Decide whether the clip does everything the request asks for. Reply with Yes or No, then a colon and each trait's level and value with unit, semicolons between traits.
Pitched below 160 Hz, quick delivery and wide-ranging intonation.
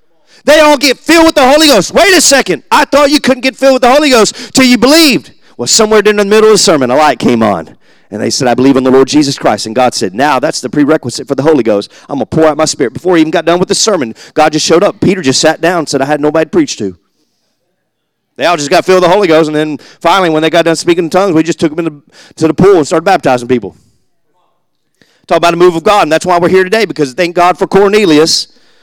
No: medium, 175 Hz; fast, 285 wpm; wide, 6.1 semitones